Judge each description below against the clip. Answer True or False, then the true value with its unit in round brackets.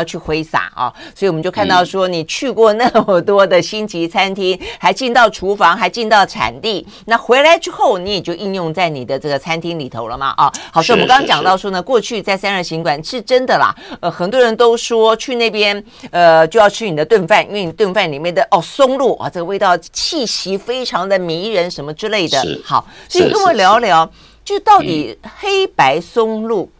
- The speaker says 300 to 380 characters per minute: True (310 characters per minute)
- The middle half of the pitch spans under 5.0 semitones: False (5.3 semitones)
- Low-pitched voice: False (200 Hz)